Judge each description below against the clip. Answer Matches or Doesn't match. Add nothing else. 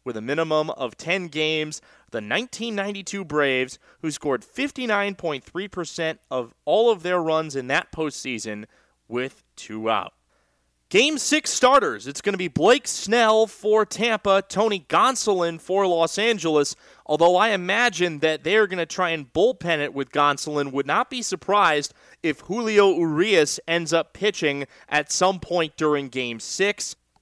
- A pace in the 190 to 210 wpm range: Doesn't match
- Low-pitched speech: Doesn't match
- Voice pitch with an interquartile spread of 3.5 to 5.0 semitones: Doesn't match